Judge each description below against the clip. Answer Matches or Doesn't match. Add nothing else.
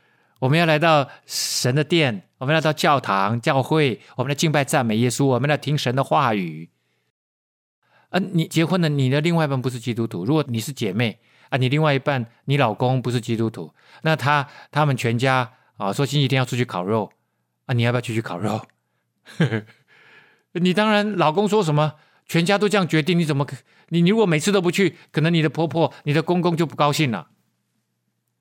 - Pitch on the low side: Doesn't match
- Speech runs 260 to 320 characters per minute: Matches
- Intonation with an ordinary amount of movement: Matches